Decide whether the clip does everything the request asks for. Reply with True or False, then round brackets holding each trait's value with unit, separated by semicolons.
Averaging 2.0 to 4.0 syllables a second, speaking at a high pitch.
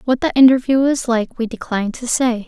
False (5.6 syllables/s; 245 Hz)